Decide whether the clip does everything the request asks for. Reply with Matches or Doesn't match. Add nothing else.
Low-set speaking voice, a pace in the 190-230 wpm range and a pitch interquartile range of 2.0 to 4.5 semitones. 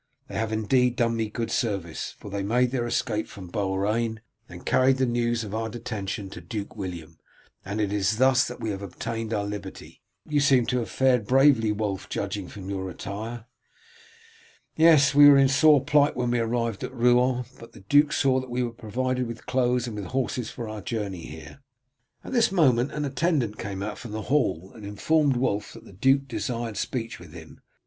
Matches